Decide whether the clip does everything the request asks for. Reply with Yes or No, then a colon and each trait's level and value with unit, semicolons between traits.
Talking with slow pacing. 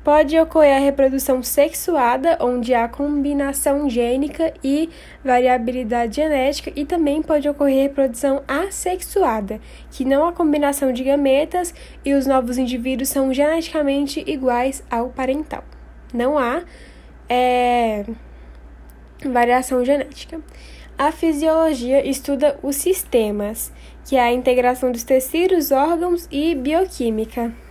Yes: slow, 115 wpm